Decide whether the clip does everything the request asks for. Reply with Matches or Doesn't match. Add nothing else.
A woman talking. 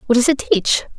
Matches